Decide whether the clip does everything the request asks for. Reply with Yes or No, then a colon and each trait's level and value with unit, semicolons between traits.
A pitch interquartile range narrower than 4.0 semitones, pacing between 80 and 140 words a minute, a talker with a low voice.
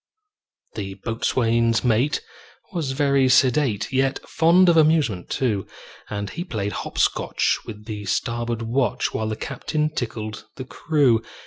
No: average, 4.6 semitones; slow, 135 wpm; low, 120 Hz